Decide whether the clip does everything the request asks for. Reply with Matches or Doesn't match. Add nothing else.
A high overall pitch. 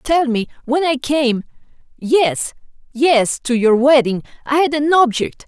Matches